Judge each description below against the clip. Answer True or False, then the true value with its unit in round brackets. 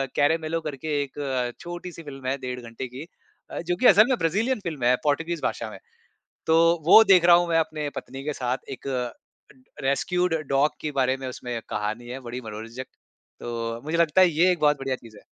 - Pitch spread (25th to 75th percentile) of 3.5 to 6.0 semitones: True (4.8 semitones)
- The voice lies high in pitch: False (145 Hz)